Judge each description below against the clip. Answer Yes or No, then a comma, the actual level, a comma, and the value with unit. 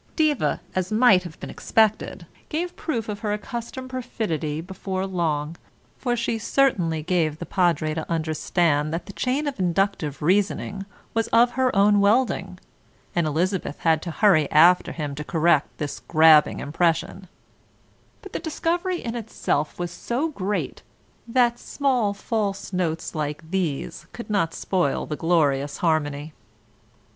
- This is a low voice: No, medium, 185 Hz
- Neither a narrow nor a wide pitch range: No, wide, 6.2 semitones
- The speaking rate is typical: Yes, average, 145 wpm